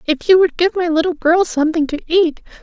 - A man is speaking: No, female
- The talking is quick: Yes, fast, 230 wpm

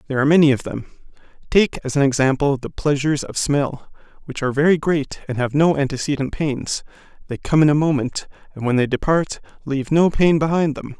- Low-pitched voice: No, medium, 145 Hz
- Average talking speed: Yes, average, 195 wpm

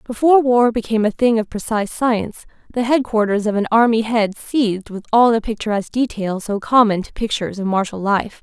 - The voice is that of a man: No, female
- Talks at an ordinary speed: Yes, average, 190 wpm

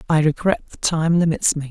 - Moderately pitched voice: Yes, medium, 160 Hz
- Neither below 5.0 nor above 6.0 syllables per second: Yes, 5.5 syllables/s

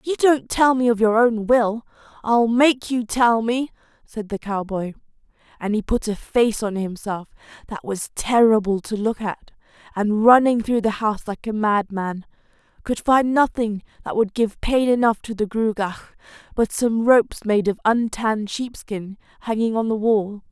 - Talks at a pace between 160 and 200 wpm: Yes, average, 175 wpm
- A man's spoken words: No, female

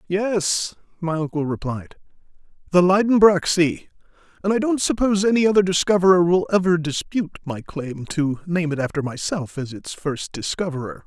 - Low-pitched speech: No, medium, 170 Hz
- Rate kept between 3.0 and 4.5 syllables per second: No, 5.1 syllables/s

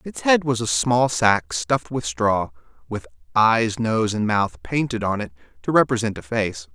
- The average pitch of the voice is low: Yes, low, 110 Hz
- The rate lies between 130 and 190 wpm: Yes, average, 185 wpm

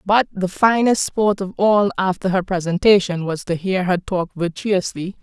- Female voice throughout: Yes, female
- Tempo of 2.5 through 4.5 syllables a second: Yes, 4.4 syllables/s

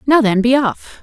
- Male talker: No, female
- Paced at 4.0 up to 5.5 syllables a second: Yes, 4.6 syllables/s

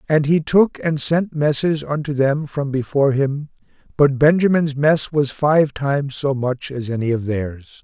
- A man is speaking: Yes, male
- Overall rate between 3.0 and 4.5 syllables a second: Yes, 4.3 syllables/s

